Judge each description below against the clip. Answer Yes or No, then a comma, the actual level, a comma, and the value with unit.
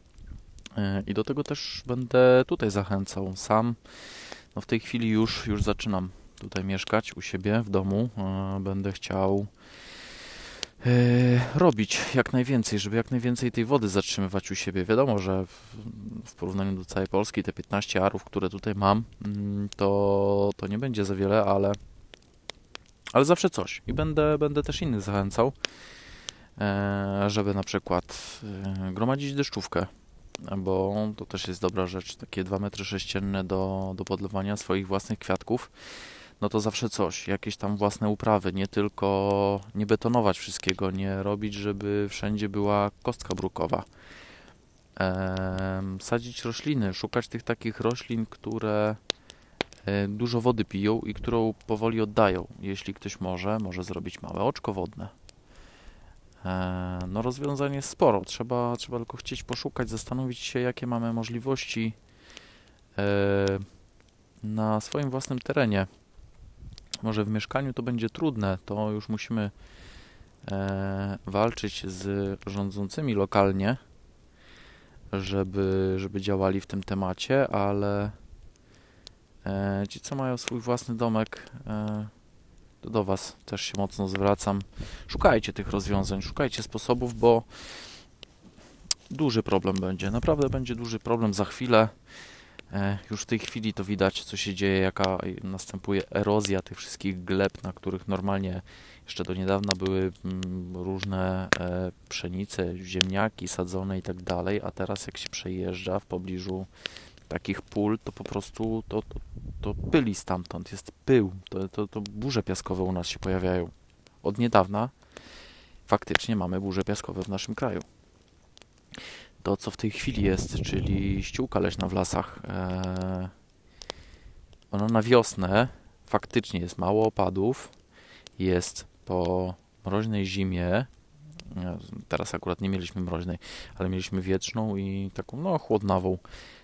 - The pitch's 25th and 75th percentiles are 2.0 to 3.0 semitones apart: Yes, average, 2.7 semitones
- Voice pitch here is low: Yes, low, 100 Hz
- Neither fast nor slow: Yes, average, 130 wpm